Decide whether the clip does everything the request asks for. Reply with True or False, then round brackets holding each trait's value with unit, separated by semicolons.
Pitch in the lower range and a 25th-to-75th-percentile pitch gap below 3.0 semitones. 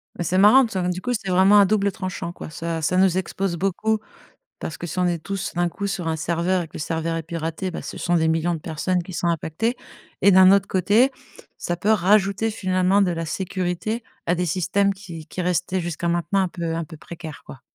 False (180 Hz; 2.6 semitones)